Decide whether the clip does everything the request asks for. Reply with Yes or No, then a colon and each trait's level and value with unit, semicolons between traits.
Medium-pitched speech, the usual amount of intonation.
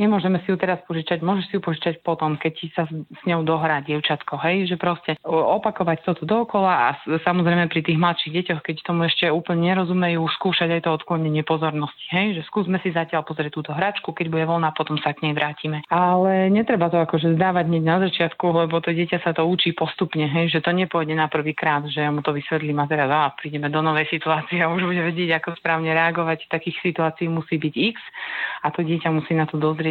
No: medium, 165 Hz; narrow, 2.0 semitones